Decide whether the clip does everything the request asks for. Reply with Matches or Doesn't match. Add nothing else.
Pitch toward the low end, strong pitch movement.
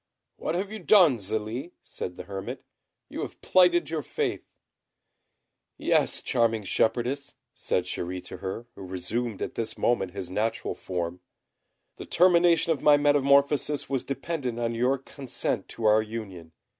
Matches